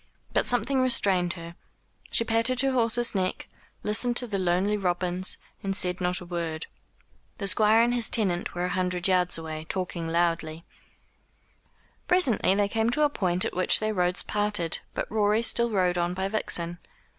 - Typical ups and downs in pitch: Yes, average, 4.0 semitones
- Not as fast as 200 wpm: Yes, average, 170 wpm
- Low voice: No, high, 190 Hz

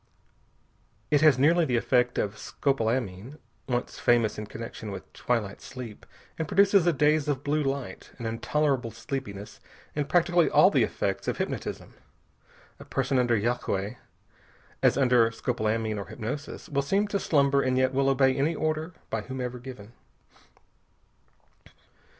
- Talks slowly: No, average, 145 wpm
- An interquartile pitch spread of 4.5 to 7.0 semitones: No, average, 4.1 semitones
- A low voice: Yes, low, 130 Hz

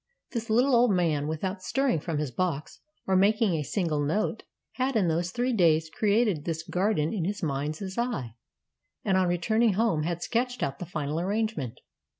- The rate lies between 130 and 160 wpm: No, average, 175 wpm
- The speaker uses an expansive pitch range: Yes, wide, 5.7 semitones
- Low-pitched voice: No, medium, 185 Hz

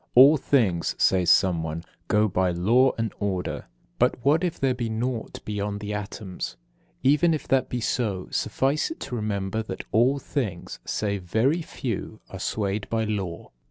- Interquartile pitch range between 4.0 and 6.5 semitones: Yes, average, 5.0 semitones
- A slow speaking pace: No, average, 160 wpm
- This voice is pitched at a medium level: No, low, 110 Hz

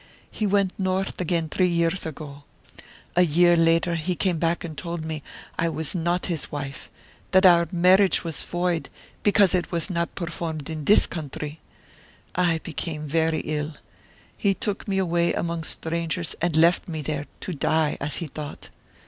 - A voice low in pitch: No, medium, 170 Hz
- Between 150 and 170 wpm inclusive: Yes, average, 165 wpm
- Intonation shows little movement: Yes, narrow, 2.3 semitones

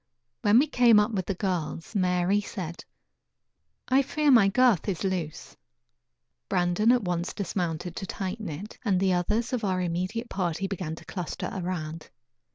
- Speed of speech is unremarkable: Yes, average, 160 wpm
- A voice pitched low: No, high, 190 Hz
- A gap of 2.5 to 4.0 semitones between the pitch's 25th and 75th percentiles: Yes, average, 3.3 semitones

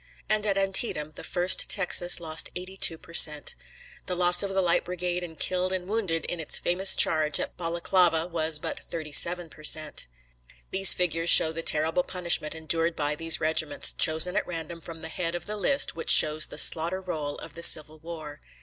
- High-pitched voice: No, medium, 170 Hz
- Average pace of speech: Yes, average, 185 wpm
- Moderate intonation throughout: No, narrow, 2.3 semitones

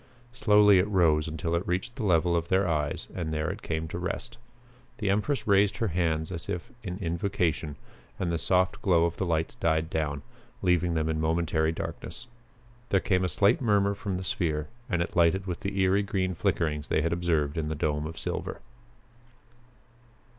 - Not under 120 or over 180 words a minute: No, average, 190 wpm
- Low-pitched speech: Yes, very low, 85 Hz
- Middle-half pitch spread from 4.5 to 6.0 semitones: No, average, 3.4 semitones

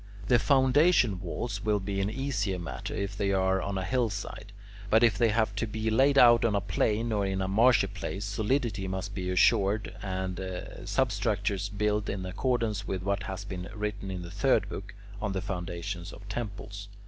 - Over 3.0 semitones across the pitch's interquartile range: No, narrow, 2.6 semitones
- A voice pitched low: Yes, low, 100 Hz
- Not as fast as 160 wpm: No, average, 185 wpm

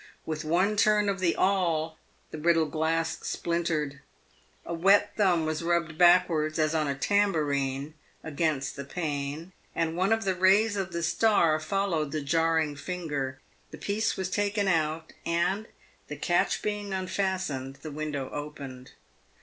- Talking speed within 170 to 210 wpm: No, average, 155 wpm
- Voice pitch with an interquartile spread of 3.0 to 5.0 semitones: Yes, average, 3.7 semitones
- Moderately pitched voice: Yes, medium, 165 Hz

